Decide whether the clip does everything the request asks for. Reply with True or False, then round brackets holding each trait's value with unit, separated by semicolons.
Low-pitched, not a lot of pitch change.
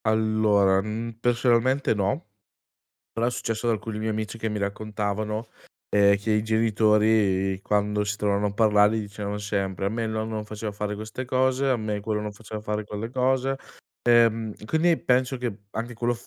True (110 Hz; 2.0 semitones)